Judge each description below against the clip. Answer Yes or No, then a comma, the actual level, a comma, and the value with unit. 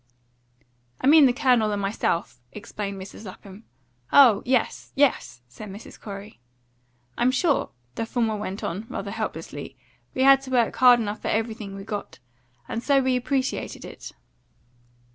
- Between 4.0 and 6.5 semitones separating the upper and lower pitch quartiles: Yes, average, 4.3 semitones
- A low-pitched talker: No, high, 225 Hz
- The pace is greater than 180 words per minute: No, average, 150 wpm